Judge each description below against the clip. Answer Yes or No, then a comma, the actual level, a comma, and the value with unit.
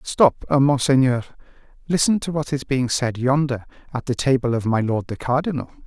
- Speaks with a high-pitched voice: No, low, 135 Hz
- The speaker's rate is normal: Yes, average, 175 wpm